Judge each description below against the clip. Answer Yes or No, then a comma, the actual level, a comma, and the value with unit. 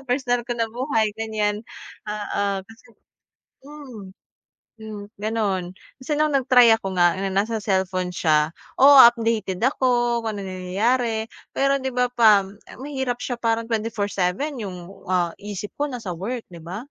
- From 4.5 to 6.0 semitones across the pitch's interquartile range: No, average, 4.1 semitones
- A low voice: No, high, 220 Hz